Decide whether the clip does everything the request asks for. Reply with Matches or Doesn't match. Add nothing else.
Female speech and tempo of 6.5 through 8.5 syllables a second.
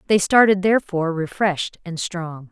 Doesn't match